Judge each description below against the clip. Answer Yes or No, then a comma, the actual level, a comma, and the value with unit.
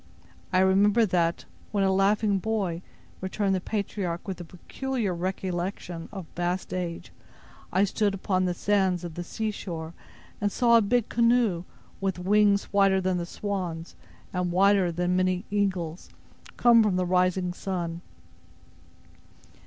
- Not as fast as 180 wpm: Yes, average, 145 wpm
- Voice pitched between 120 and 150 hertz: No, high, 190 Hz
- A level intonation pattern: Yes, narrow, 2.3 semitones